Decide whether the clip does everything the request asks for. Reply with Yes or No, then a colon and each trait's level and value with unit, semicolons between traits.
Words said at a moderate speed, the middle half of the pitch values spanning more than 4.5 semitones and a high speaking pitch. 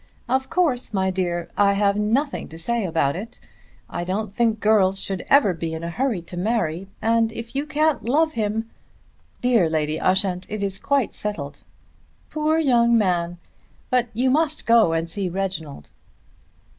Yes: average, 170 wpm; average, 5.2 semitones; high, 210 Hz